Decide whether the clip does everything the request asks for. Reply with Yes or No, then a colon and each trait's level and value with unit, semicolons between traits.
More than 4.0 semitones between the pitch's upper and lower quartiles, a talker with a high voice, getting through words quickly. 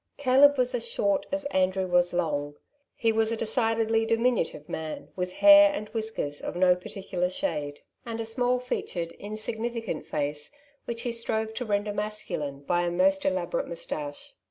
No: wide, 5.5 semitones; high, 220 Hz; average, 165 wpm